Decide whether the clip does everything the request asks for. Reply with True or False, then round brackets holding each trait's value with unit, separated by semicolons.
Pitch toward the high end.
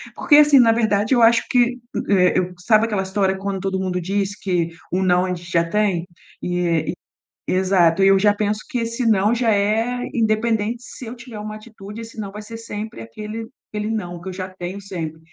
True (205 Hz)